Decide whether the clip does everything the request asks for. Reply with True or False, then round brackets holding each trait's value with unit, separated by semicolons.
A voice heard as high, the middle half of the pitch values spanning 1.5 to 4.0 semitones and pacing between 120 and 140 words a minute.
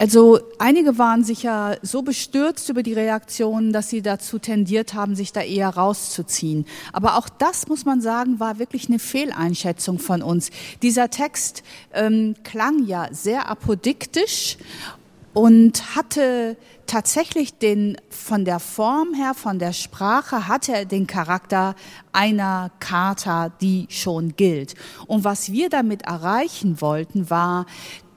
False (215 Hz; 4.4 semitones; 135 wpm)